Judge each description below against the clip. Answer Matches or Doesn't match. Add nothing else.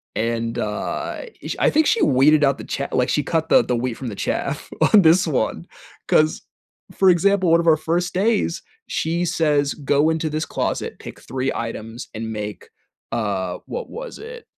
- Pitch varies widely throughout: Matches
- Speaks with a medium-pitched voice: Matches